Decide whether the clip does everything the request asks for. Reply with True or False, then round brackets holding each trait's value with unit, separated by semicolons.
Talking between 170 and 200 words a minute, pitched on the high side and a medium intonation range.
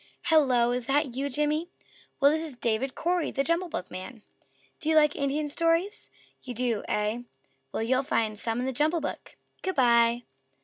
True (175 wpm; 275 Hz; 4.7 semitones)